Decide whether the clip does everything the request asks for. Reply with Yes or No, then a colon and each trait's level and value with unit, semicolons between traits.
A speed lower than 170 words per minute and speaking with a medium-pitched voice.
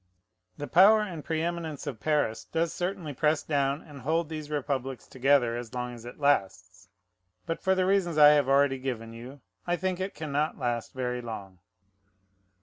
No: average, 175 wpm; medium, 145 Hz